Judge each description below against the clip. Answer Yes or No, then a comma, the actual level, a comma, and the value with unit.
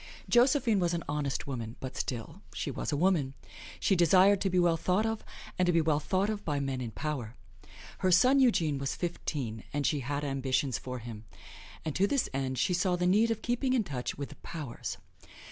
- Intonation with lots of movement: Yes, wide, 6.1 semitones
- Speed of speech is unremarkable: No, fast, 210 wpm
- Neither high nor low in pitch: Yes, medium, 160 Hz